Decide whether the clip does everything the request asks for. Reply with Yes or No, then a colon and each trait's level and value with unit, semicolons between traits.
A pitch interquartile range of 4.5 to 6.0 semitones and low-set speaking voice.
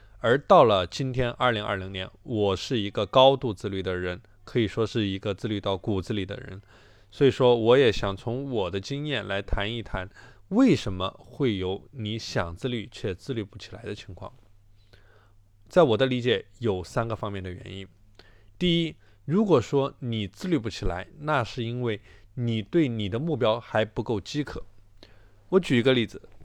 No: average, 3.9 semitones; low, 110 Hz